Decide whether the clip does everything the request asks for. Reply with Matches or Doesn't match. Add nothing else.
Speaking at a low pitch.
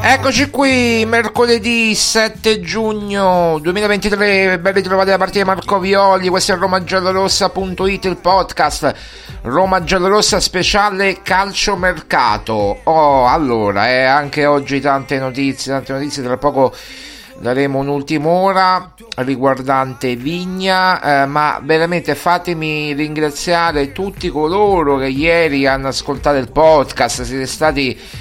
Doesn't match